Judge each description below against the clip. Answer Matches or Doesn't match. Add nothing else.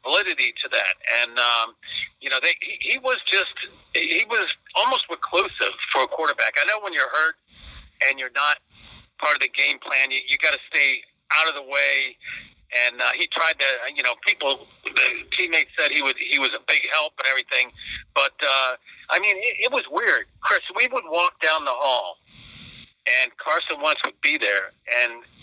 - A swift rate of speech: Doesn't match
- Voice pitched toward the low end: Doesn't match